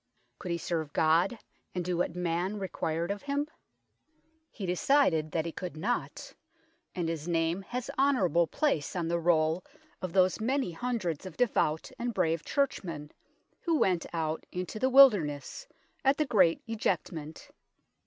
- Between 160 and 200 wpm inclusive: No, average, 150 wpm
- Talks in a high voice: No, medium, 180 Hz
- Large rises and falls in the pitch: Yes, wide, 5.7 semitones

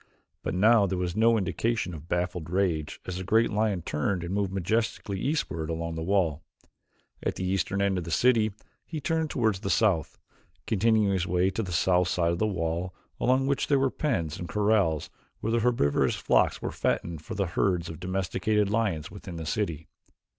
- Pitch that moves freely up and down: No, average, 4.2 semitones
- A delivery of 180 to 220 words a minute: Yes, average, 190 wpm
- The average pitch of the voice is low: Yes, very low, 95 Hz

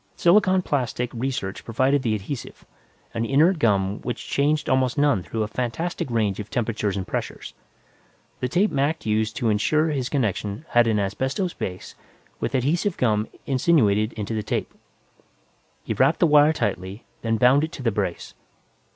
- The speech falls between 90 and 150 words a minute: No, average, 160 wpm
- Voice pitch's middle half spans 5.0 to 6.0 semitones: Yes, wide, 5.4 semitones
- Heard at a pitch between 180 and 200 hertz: No, low, 120 Hz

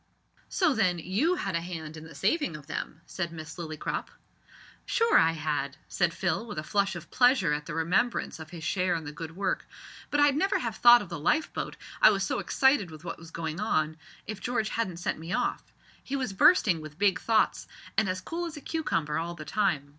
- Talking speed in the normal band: No, fast, 215 wpm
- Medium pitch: Yes, medium, 180 Hz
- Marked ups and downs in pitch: Yes, wide, 6.2 semitones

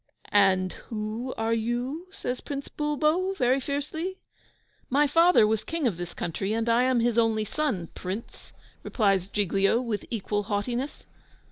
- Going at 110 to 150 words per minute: Yes, average, 145 wpm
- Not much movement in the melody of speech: No, wide, 5.5 semitones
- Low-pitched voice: No, high, 235 Hz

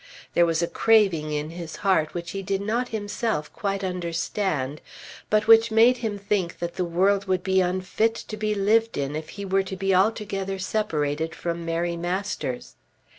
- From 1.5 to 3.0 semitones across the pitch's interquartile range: No, average, 3.7 semitones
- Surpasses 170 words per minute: Yes, average, 180 wpm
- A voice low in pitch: No, high, 190 Hz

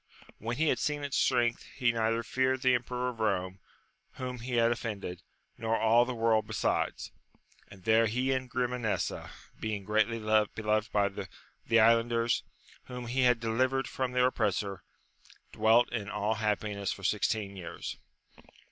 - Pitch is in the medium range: No, low, 115 Hz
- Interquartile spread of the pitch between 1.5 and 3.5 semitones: Yes, average, 2.7 semitones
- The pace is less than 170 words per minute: Yes, average, 155 wpm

